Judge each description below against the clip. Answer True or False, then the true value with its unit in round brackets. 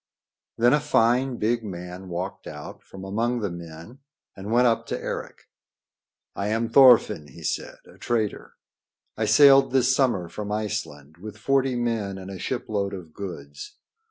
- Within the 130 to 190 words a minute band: True (155 wpm)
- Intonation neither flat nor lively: True (4.6 semitones)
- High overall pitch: False (105 Hz)